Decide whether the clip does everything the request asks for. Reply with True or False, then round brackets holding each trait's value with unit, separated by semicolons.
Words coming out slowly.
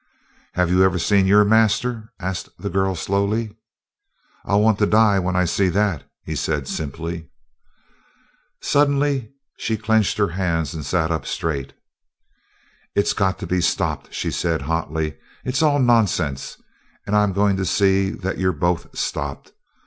False (150 wpm)